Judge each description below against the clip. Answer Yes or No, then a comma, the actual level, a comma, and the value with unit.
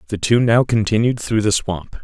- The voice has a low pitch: Yes, low, 110 Hz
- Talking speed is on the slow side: No, fast, 205 wpm